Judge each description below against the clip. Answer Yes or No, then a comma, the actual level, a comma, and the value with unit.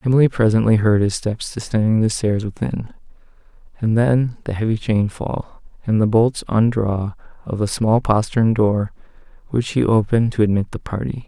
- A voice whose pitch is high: No, low, 110 Hz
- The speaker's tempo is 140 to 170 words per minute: Yes, average, 165 wpm